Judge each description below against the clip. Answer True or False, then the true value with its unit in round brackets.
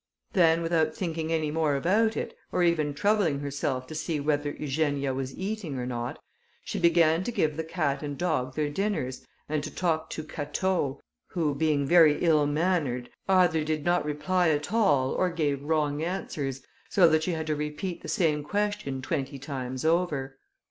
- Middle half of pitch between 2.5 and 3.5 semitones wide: True (3.2 semitones)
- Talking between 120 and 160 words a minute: False (175 wpm)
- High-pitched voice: False (155 Hz)